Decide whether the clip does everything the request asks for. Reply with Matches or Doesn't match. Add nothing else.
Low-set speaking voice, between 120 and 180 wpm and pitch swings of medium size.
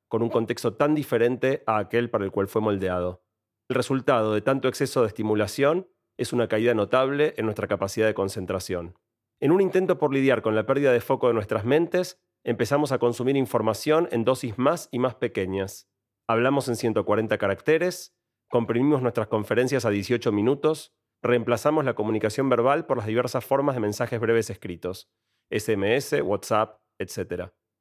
Matches